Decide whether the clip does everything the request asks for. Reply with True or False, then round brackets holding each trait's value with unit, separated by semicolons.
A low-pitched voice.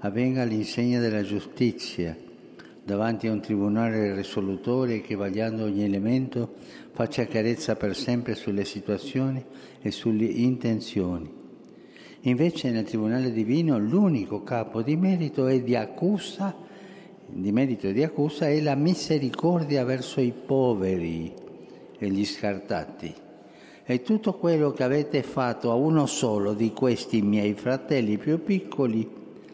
True (120 Hz)